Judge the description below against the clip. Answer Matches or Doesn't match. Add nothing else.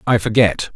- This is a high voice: Doesn't match